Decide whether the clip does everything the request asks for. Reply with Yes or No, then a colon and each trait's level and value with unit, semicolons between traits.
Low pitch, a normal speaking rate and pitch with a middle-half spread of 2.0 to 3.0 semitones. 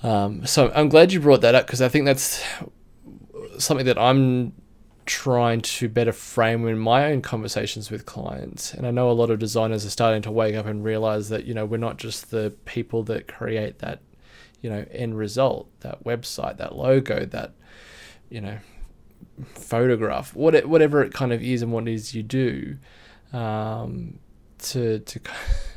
Yes: low, 115 Hz; average, 175 wpm; narrow, 2.6 semitones